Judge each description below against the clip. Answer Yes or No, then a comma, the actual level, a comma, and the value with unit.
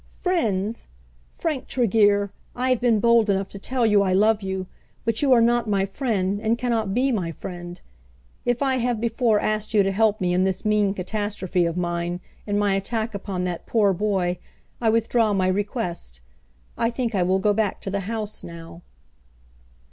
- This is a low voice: No, high, 205 Hz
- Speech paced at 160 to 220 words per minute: Yes, average, 185 wpm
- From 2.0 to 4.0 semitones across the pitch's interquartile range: Yes, average, 3.3 semitones